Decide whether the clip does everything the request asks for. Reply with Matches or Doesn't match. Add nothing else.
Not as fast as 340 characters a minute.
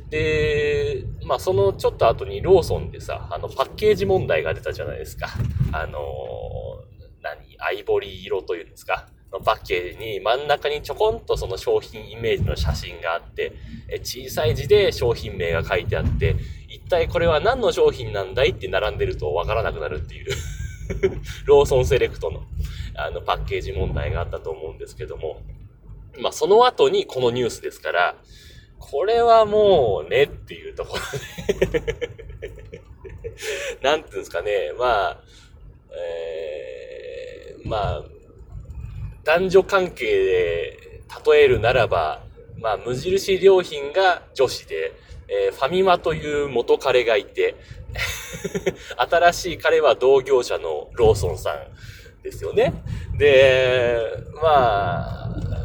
Matches